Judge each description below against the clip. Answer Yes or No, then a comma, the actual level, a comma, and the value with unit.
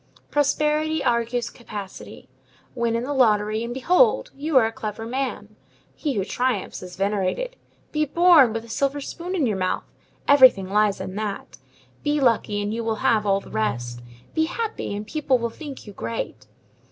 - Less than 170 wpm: No, average, 175 wpm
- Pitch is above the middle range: Yes, high, 235 Hz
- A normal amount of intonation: No, wide, 5.7 semitones